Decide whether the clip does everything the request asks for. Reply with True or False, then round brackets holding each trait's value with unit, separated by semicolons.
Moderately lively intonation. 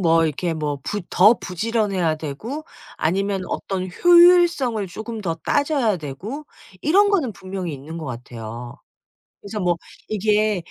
False (6.0 semitones)